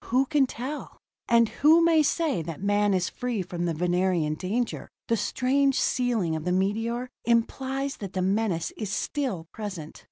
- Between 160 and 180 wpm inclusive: Yes, average, 165 wpm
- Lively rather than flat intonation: Yes, wide, 5.9 semitones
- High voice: Yes, high, 220 Hz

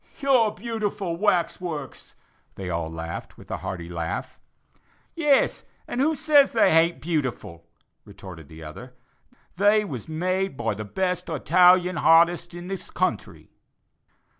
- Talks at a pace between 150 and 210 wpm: No, slow, 135 wpm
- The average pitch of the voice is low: No, medium, 170 Hz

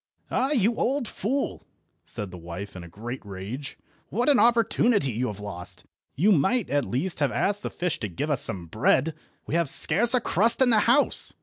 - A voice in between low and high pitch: Yes, medium, 155 Hz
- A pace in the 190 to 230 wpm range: Yes, average, 200 wpm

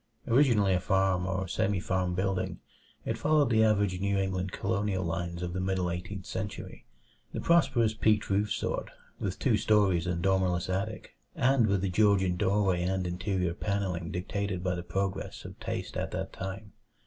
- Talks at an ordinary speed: Yes, average, 170 wpm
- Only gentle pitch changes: Yes, narrow, 2.2 semitones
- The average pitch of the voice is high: No, very low, 95 Hz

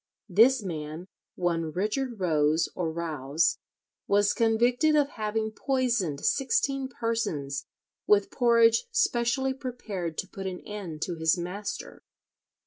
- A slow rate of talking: Yes, slow, 120 wpm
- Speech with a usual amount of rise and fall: No, wide, 6.2 semitones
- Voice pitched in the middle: No, high, 205 Hz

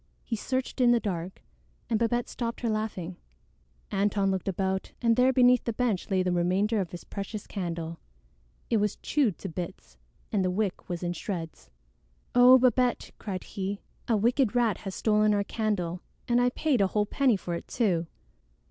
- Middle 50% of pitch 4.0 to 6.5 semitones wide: Yes, average, 4.4 semitones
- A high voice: Yes, high, 205 Hz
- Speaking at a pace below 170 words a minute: No, average, 180 wpm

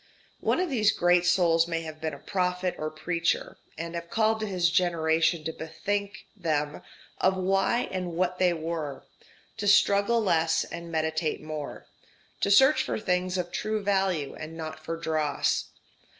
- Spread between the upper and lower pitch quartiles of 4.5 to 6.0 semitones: No, average, 3.2 semitones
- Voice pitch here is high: No, medium, 175 Hz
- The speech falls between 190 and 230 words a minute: No, average, 165 wpm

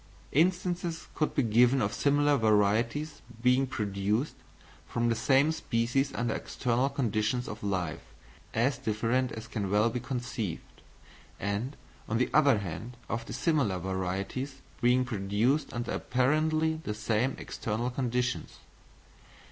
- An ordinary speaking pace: No, slow, 125 wpm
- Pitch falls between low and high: No, low, 120 Hz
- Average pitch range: Yes, average, 4.2 semitones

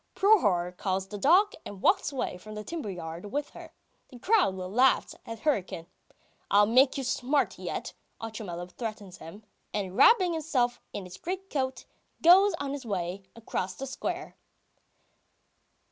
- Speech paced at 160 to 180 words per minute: No, average, 145 wpm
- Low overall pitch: No, high, 225 Hz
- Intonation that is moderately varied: No, wide, 7.1 semitones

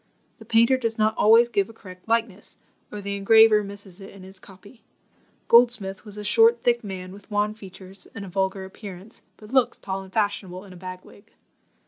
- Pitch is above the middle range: Yes, high, 205 Hz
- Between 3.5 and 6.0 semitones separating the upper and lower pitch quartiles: No, average, 2.7 semitones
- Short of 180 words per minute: No, average, 195 wpm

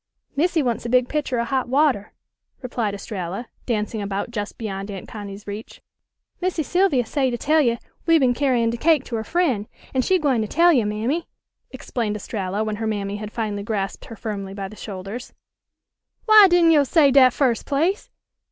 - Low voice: No, high, 235 Hz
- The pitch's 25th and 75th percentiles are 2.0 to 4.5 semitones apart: No, wide, 5.5 semitones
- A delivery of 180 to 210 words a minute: Yes, average, 190 wpm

